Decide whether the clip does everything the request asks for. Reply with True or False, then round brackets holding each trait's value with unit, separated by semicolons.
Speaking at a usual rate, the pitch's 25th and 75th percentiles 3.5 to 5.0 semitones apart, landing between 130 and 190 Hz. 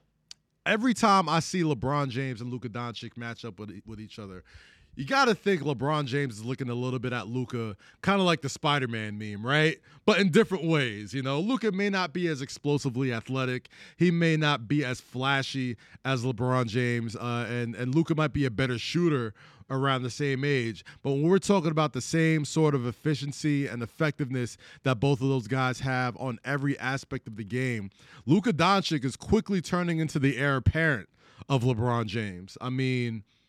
True (195 wpm; 4.4 semitones; 135 Hz)